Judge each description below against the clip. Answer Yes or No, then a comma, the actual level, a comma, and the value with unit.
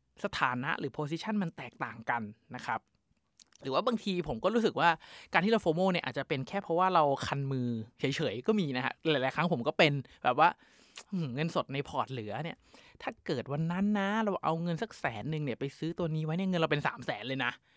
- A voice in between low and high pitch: Yes, medium, 155 Hz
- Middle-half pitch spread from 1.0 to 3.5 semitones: No, average, 5.0 semitones